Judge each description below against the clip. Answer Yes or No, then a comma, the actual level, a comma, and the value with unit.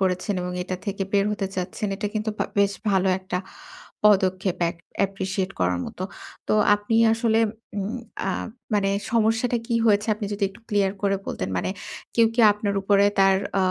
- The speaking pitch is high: Yes, high, 200 Hz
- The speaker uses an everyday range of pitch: No, narrow, 1.9 semitones